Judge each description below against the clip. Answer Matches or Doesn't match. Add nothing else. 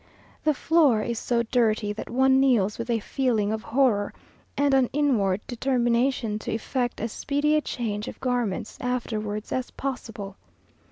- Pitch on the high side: Matches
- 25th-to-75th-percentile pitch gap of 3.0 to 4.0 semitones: Matches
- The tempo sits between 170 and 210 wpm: Doesn't match